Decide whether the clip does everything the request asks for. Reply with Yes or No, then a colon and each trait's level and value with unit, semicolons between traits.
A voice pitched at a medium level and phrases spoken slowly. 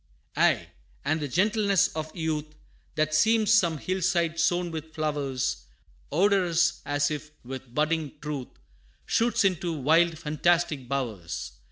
Yes: medium, 160 Hz; slow, 130 wpm